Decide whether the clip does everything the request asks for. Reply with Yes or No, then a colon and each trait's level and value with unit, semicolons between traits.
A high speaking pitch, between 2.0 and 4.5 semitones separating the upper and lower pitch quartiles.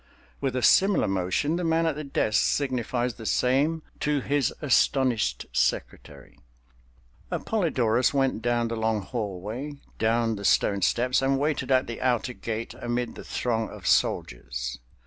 No: low, 120 Hz; average, 3.8 semitones